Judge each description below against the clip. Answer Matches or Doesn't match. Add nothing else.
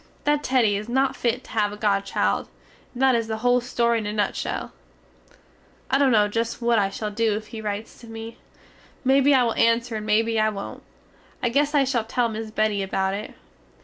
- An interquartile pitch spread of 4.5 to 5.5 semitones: Doesn't match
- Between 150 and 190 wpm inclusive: Doesn't match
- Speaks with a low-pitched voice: Doesn't match